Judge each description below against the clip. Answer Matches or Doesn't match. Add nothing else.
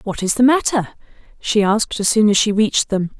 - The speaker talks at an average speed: Doesn't match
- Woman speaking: Matches